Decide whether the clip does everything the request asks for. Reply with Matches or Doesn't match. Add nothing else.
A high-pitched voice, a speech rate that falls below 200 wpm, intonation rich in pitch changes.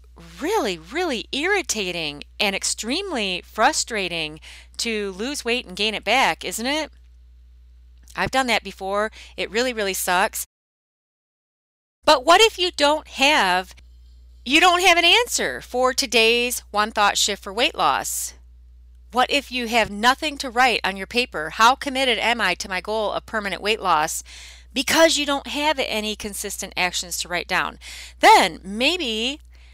Matches